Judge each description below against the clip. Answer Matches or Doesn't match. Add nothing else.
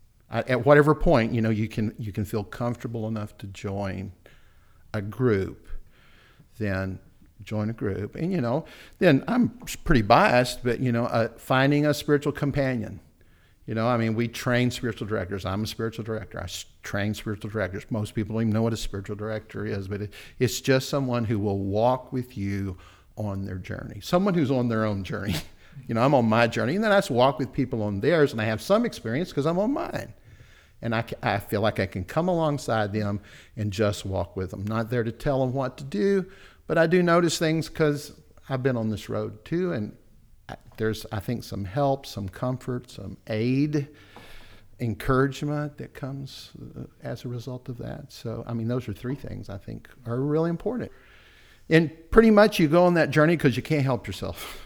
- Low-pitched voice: Matches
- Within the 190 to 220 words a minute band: Matches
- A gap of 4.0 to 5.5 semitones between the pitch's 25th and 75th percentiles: Matches